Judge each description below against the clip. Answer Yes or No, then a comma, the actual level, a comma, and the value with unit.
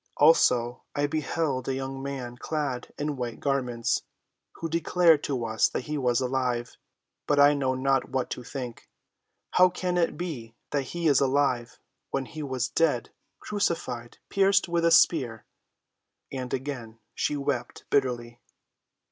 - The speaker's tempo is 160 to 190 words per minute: No, average, 140 wpm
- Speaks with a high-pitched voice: No, low, 135 Hz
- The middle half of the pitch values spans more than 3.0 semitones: Yes, average, 3.6 semitones